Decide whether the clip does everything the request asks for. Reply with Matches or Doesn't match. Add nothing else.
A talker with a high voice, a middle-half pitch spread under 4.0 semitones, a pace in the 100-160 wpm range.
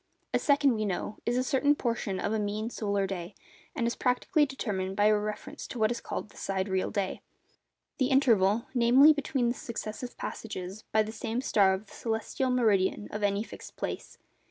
Doesn't match